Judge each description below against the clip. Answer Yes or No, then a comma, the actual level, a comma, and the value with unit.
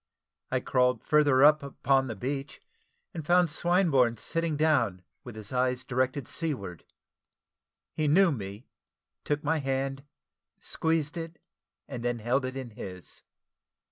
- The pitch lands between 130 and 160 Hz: Yes, low, 135 Hz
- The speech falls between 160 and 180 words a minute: No, slow, 135 wpm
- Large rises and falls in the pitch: No, average, 3.9 semitones